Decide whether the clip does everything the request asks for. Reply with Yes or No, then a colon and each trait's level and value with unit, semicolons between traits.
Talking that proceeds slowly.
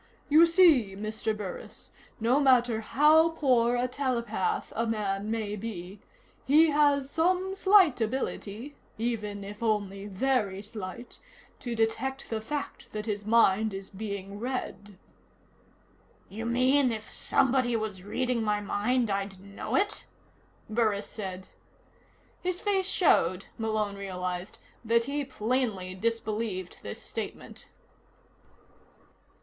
Yes: slow, 120 wpm